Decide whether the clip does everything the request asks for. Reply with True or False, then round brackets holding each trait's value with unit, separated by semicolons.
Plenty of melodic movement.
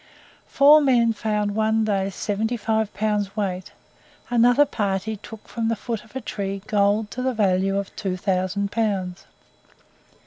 False (2.4 semitones)